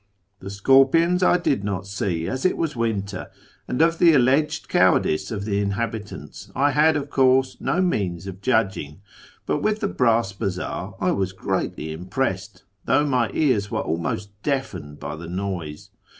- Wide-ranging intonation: Yes, wide, 6.5 semitones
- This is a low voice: Yes, low, 105 Hz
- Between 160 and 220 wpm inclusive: Yes, average, 165 wpm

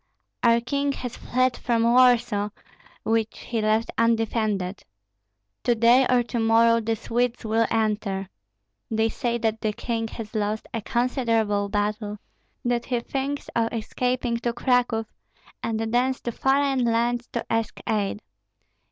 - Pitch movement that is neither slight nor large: No, narrow, 1.8 semitones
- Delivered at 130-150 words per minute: Yes, average, 140 wpm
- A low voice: No, high, 230 Hz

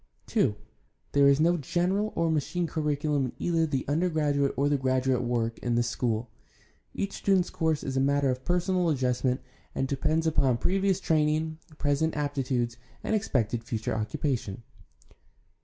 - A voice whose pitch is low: No, medium, 145 Hz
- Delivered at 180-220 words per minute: No, average, 155 wpm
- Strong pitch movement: No, average, 4.2 semitones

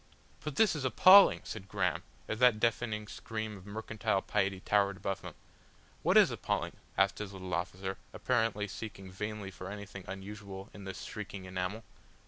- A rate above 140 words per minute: Yes, average, 160 wpm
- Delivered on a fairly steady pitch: Yes, narrow, 2.3 semitones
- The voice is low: Yes, low, 100 Hz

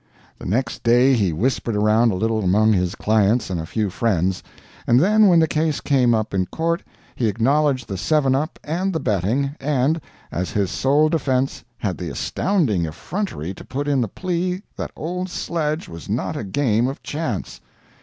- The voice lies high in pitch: No, low, 125 Hz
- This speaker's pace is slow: No, average, 185 wpm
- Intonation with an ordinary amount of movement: No, wide, 6.6 semitones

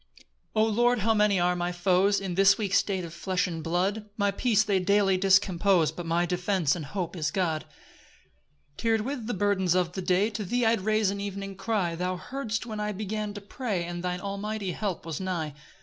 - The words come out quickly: Yes, fast, 210 wpm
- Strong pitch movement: No, average, 2.8 semitones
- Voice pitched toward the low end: No, high, 195 Hz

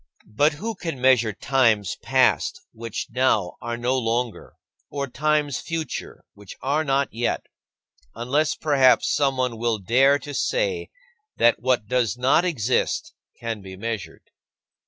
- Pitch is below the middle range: Yes, low, 130 Hz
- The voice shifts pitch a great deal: No, average, 3.9 semitones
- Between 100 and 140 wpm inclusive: Yes, slow, 135 wpm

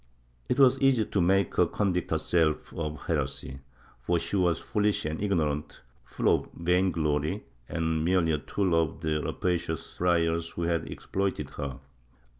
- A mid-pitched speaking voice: No, very low, 85 Hz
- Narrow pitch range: No, average, 3.3 semitones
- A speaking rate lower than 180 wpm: Yes, average, 160 wpm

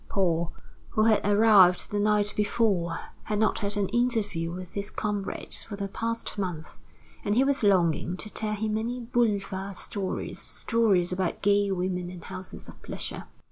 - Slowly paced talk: No, average, 165 wpm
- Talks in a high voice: Yes, high, 205 Hz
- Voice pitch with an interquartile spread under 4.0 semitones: Yes, average, 2.9 semitones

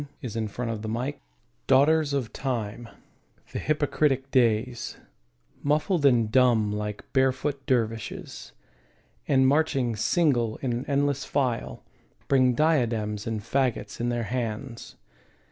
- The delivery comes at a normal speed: No, slow, 115 wpm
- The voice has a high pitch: No, low, 125 Hz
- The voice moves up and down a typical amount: Yes, average, 3.5 semitones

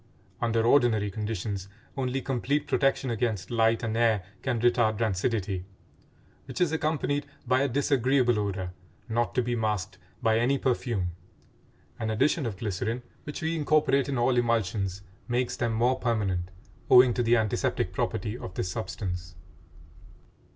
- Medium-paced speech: Yes, average, 145 wpm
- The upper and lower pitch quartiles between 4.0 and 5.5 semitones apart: No, average, 3.4 semitones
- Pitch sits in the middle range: No, low, 115 Hz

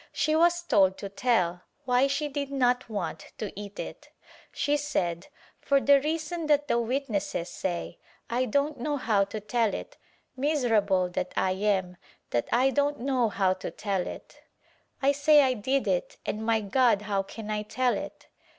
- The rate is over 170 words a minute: Yes, average, 180 wpm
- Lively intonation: Yes, wide, 5.9 semitones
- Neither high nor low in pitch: No, high, 235 Hz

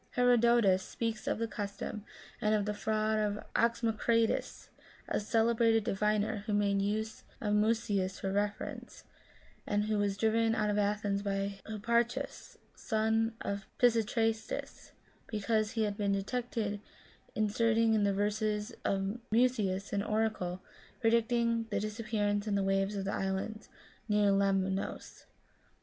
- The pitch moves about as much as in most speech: No, narrow, 1.9 semitones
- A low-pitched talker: No, high, 215 Hz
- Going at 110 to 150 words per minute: Yes, slow, 135 wpm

